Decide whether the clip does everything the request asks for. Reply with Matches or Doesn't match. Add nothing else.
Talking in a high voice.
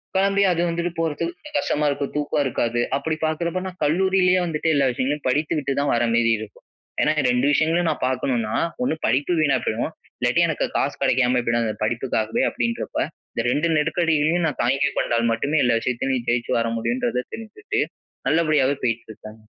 Doesn't match